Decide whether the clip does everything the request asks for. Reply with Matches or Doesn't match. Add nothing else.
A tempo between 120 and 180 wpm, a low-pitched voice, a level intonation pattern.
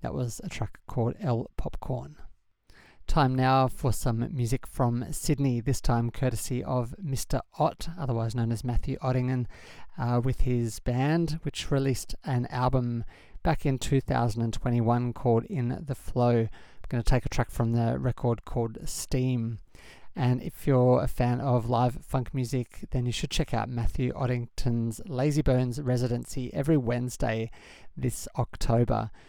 Matches